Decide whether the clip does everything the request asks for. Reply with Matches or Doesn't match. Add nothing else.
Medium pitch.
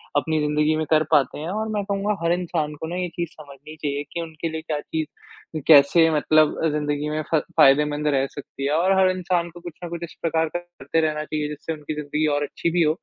Matches